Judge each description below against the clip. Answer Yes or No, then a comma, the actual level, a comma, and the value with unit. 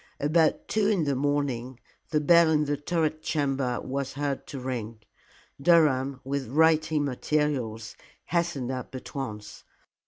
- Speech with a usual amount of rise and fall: Yes, average, 3.2 semitones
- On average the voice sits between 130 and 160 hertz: Yes, medium, 140 Hz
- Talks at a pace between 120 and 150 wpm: Yes, slow, 135 wpm